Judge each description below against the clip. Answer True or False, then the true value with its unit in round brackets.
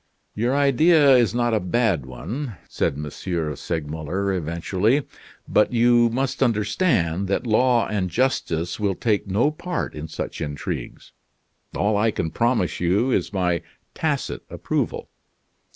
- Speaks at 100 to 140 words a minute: True (135 wpm)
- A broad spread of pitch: True (6.1 semitones)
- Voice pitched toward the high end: False (105 Hz)